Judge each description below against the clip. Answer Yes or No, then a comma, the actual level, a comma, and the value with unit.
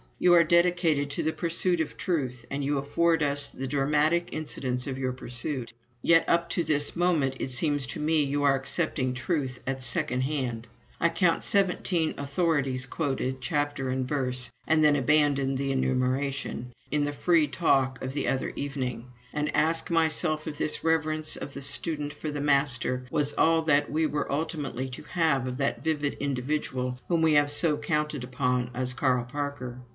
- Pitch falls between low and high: Yes, medium, 145 Hz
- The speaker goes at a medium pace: Yes, average, 175 wpm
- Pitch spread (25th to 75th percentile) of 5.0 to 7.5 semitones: No, average, 3.2 semitones